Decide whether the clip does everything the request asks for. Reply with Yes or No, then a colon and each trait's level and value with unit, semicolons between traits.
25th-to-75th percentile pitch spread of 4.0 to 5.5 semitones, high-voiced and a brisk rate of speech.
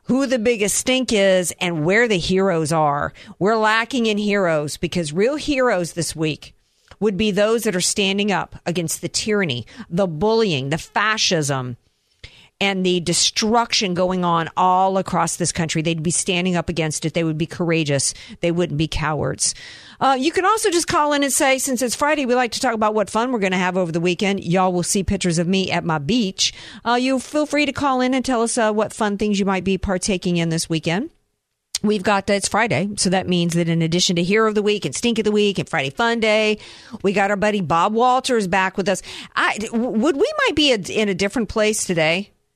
Yes: average, 4.5 semitones; high, 195 Hz; fast, 220 wpm